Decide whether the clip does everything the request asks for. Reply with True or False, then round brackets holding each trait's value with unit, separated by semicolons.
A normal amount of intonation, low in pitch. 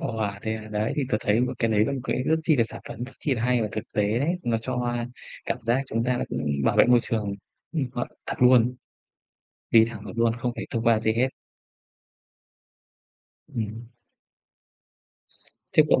False (2.2 semitones; 115 Hz)